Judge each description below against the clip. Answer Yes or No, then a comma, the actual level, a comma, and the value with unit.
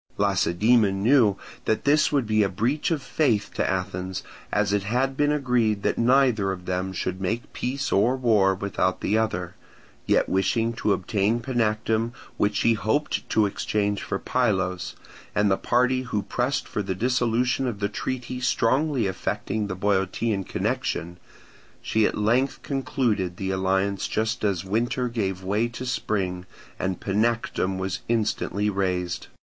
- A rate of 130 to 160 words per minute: Yes, average, 150 wpm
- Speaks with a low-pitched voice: Yes, low, 105 Hz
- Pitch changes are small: No, average, 4.1 semitones